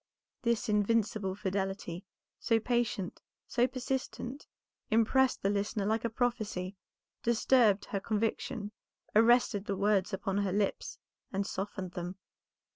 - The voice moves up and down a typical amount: Yes, average, 3.1 semitones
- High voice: Yes, high, 210 Hz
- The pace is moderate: No, slow, 120 wpm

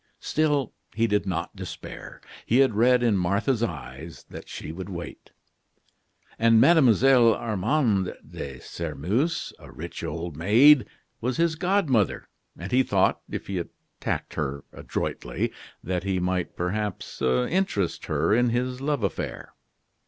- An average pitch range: No, wide, 6.4 semitones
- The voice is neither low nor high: No, low, 105 Hz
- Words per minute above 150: No, slow, 135 wpm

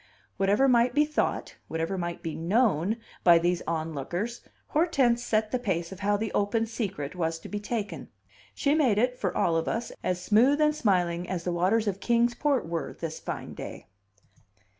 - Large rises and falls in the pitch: Yes, wide, 5.7 semitones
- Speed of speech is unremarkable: Yes, average, 185 wpm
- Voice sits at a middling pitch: No, high, 200 Hz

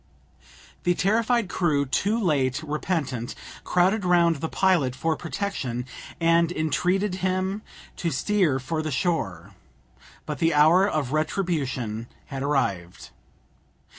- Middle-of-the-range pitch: Yes, medium, 160 Hz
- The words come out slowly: Yes, slow, 115 wpm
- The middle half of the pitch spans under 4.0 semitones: No, average, 5.3 semitones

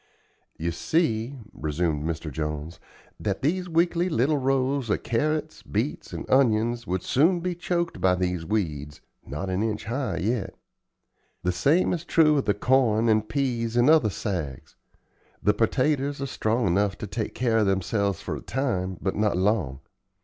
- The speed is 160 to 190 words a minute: Yes, average, 165 wpm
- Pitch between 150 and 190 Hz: No, low, 110 Hz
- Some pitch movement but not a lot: No, wide, 6.9 semitones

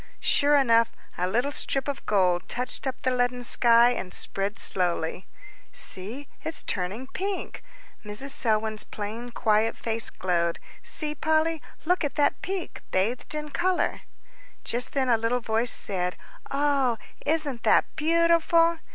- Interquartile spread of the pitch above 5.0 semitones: Yes, wide, 5.4 semitones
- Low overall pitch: No, high, 245 Hz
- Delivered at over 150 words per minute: No, average, 140 wpm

